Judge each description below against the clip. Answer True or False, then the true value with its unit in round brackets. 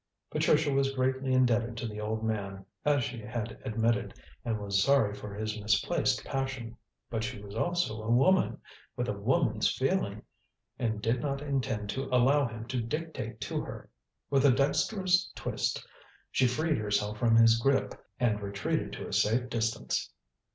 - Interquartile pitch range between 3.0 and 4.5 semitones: True (3.8 semitones)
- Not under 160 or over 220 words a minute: True (165 wpm)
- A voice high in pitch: False (115 Hz)